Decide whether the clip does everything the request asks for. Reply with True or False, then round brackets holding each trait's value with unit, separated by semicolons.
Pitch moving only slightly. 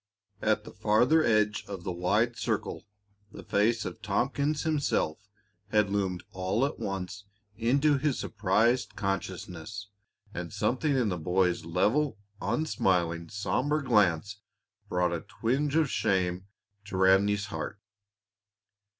False (4.8 semitones)